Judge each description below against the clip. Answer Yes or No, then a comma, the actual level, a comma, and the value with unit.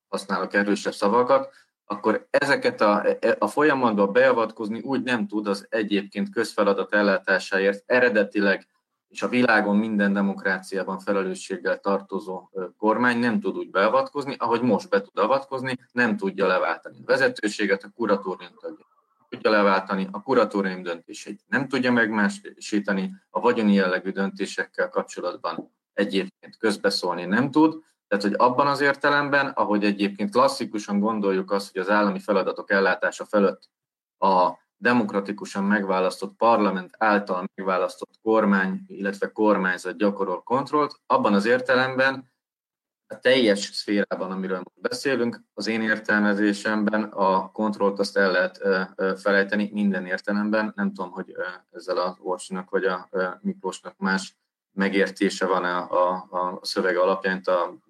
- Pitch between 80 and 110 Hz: Yes, low, 105 Hz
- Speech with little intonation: No, average, 3.3 semitones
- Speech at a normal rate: Yes, average, 125 wpm